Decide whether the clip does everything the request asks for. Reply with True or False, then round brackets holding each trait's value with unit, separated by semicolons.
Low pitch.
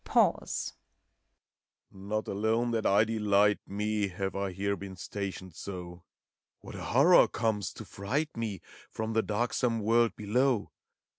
True (105 Hz)